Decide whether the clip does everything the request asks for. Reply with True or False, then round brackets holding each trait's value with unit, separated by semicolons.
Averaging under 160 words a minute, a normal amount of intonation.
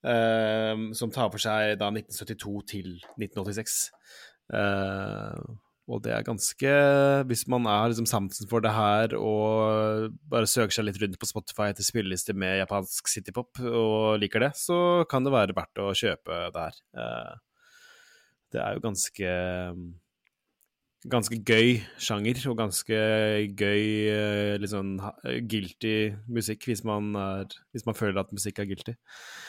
False (150 wpm; 2.1 semitones)